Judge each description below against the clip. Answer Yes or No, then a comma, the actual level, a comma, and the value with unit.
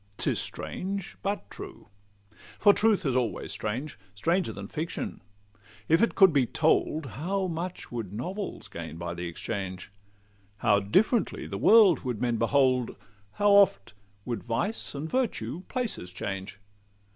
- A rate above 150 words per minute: No, slow, 135 wpm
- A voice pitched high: No, medium, 140 Hz